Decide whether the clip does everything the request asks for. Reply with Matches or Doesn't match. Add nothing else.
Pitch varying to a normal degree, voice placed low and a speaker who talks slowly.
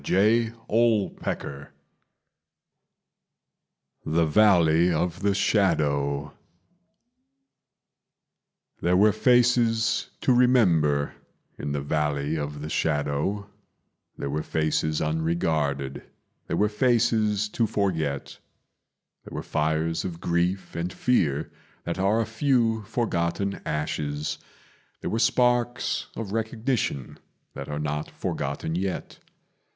Doesn't match